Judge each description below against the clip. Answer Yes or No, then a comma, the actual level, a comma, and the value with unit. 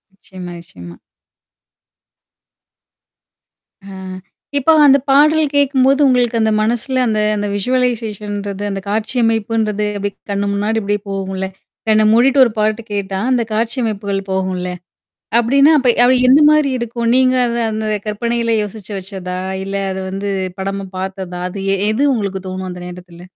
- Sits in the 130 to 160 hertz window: No, high, 215 Hz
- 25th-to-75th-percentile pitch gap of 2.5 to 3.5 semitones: No, average, 3.9 semitones